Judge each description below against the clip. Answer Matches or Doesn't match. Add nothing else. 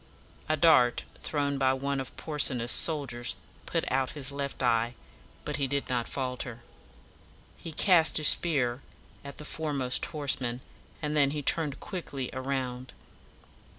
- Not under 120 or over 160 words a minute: Matches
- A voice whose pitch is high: Doesn't match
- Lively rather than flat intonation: Doesn't match